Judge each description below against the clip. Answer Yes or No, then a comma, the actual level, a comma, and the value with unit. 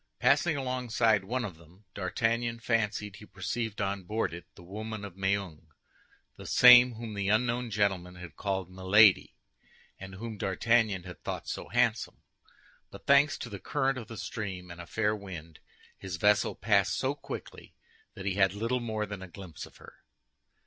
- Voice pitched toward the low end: Yes, low, 105 Hz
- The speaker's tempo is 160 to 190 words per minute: Yes, average, 170 wpm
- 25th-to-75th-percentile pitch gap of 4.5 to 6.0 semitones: No, average, 3.5 semitones